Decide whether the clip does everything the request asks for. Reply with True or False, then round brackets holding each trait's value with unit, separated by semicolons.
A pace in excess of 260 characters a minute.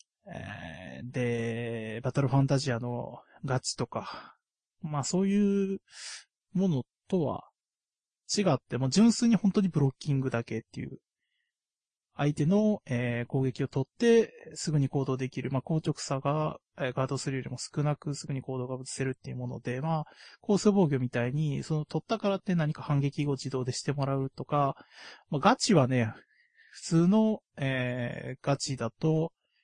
True (295 characters per minute)